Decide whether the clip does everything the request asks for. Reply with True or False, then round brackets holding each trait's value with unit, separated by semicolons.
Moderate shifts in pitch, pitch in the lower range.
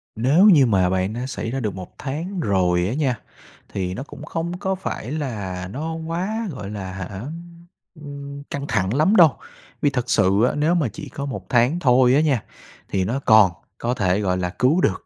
False (7.6 semitones; 130 Hz)